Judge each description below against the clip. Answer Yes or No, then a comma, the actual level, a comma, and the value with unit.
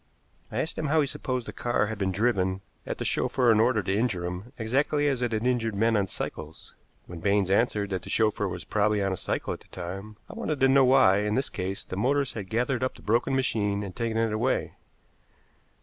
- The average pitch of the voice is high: No, low, 110 Hz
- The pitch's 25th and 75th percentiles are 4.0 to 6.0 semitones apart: Yes, average, 4.3 semitones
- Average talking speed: No, fast, 230 wpm